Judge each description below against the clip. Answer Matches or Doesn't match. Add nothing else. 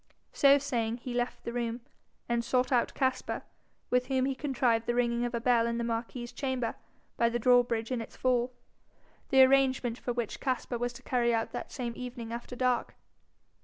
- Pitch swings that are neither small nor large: Doesn't match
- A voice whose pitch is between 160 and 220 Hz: Doesn't match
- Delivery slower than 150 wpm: Doesn't match